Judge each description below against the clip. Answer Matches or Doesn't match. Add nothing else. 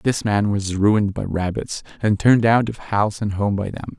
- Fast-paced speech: Matches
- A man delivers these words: Matches